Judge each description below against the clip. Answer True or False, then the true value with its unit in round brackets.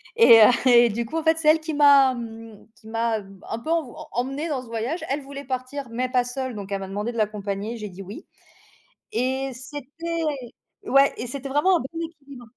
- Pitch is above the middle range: True (255 Hz)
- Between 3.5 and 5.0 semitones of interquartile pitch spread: True (3.9 semitones)